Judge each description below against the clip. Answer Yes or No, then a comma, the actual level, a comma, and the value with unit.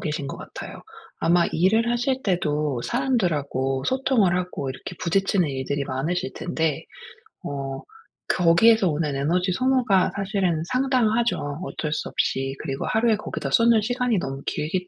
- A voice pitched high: No, medium, 180 Hz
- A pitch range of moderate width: No, wide, 7.2 semitones